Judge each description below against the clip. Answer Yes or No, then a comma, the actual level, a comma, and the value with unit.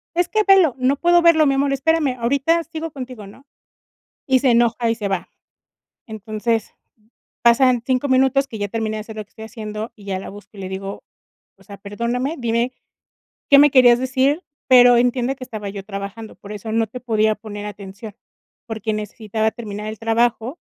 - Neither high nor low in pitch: No, high, 235 Hz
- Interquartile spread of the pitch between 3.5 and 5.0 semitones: Yes, average, 3.8 semitones